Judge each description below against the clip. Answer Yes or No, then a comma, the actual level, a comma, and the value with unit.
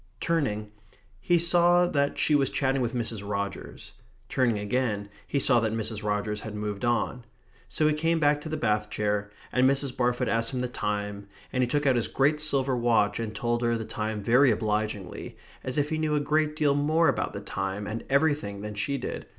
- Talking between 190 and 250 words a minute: Yes, fast, 205 wpm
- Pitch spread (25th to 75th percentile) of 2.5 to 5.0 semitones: No, wide, 5.4 semitones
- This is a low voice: Yes, low, 120 Hz